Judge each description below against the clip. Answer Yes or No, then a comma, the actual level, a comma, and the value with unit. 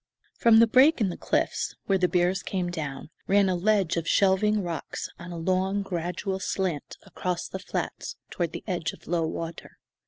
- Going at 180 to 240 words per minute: Yes, average, 185 wpm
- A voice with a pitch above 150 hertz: Yes, medium, 185 Hz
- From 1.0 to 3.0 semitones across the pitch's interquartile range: Yes, narrow, 2.4 semitones